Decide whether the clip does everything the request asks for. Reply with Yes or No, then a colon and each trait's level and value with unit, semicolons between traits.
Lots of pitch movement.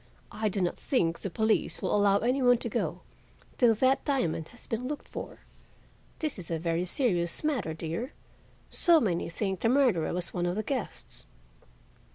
Yes: wide, 6.5 semitones